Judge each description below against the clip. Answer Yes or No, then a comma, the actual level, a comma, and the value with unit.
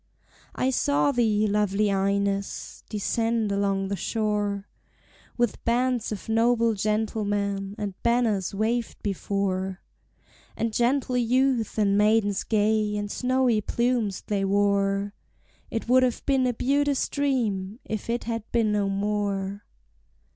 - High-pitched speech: Yes, high, 215 Hz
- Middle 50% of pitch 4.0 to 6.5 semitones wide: No, average, 2.9 semitones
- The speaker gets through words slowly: Yes, slow, 125 wpm